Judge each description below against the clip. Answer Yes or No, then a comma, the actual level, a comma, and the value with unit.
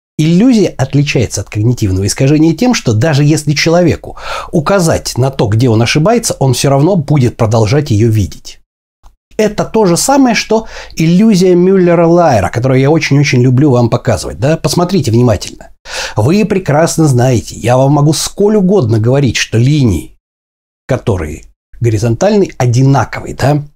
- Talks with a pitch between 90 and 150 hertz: Yes, medium, 140 Hz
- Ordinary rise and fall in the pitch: No, wide, 6.3 semitones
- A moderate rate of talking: Yes, average, 140 wpm